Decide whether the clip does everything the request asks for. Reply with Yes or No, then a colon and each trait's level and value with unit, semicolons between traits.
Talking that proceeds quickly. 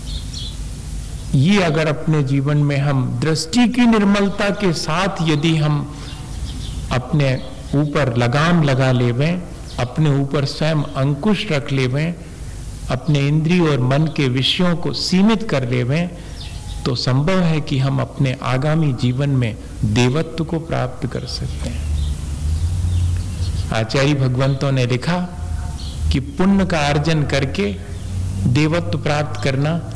No: average, 120 wpm